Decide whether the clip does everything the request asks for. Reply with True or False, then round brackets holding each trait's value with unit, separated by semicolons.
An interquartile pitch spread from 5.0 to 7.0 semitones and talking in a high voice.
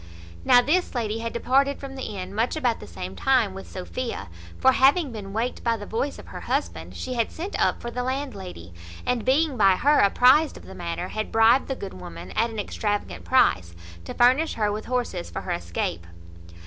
True (5.5 semitones; 230 Hz)